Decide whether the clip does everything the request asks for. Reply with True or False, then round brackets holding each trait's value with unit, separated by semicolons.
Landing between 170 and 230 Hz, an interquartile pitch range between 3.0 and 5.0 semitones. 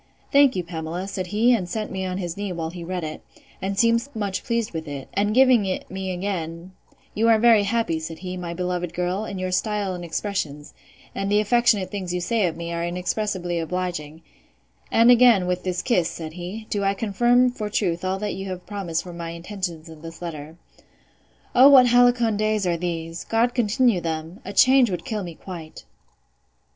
True (185 Hz; 3.9 semitones)